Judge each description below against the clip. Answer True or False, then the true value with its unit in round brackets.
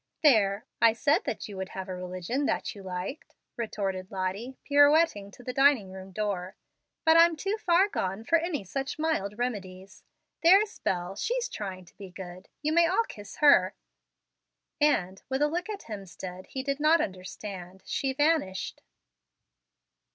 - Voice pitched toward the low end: False (215 Hz)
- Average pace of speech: True (160 wpm)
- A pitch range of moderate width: False (7.9 semitones)